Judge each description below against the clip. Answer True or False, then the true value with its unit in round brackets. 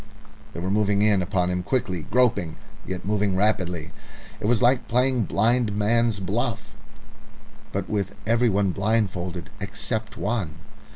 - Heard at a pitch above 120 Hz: False (105 Hz)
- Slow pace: True (125 wpm)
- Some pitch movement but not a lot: True (3.6 semitones)